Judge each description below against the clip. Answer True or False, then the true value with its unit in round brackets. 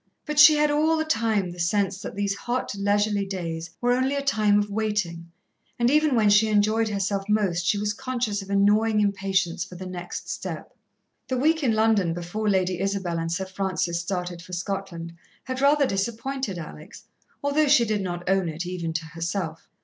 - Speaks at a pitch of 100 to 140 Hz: False (200 Hz)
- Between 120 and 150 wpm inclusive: False (190 wpm)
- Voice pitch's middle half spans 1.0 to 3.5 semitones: False (4.0 semitones)